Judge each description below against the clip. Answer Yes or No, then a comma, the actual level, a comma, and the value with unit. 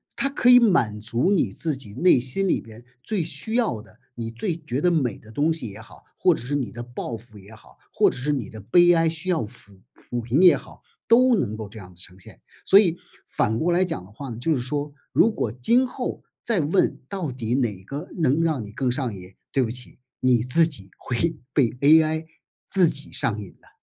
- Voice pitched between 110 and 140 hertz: Yes, low, 135 Hz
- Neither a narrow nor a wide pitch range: No, wide, 6.9 semitones